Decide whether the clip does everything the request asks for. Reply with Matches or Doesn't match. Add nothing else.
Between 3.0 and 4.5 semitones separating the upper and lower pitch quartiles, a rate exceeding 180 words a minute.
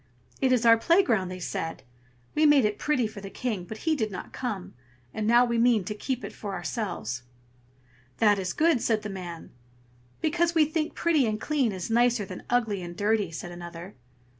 Doesn't match